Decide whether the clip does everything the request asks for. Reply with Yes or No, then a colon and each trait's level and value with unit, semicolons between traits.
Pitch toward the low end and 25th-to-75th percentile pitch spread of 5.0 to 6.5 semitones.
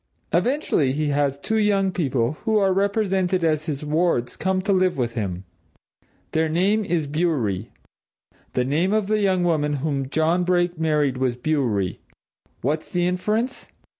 No: medium, 160 Hz; average, 5.3 semitones